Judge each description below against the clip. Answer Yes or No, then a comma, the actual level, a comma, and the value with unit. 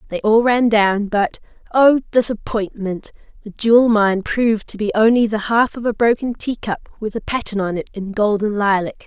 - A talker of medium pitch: No, high, 215 Hz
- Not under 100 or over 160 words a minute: No, average, 180 wpm